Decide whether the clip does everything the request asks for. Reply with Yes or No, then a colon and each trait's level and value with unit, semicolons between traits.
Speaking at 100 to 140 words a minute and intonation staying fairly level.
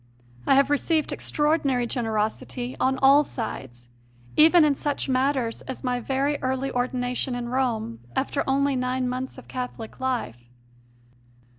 Yes: slow, 135 wpm; narrow, 2.1 semitones